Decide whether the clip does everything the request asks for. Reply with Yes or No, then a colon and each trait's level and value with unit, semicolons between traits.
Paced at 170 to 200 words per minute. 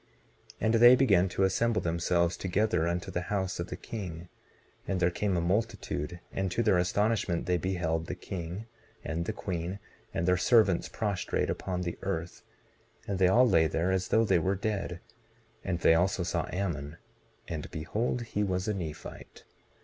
Yes: average, 175 wpm